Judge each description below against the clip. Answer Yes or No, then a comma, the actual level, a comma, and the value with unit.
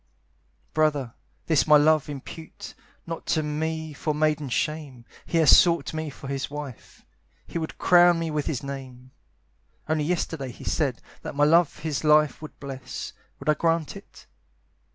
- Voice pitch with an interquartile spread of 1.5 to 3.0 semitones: Yes, narrow, 2.4 semitones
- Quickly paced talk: No, average, 160 wpm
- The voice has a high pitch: No, medium, 150 Hz